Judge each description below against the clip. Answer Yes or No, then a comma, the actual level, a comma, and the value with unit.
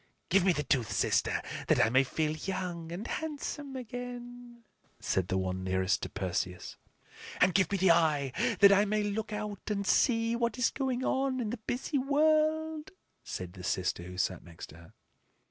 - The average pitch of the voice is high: Yes, high, 200 Hz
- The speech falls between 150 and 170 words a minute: No, average, 180 wpm